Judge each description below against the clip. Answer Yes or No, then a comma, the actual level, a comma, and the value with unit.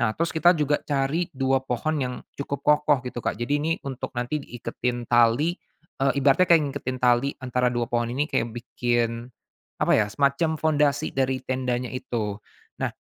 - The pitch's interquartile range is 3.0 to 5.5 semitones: Yes, average, 3.3 semitones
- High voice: No, low, 130 Hz